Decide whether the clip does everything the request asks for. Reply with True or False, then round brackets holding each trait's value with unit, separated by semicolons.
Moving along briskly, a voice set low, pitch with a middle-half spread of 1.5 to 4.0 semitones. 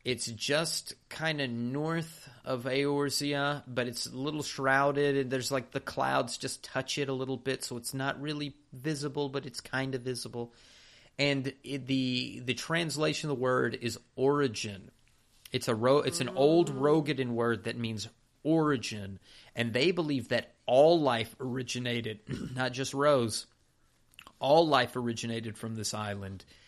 False (155 wpm; 130 Hz; 3.2 semitones)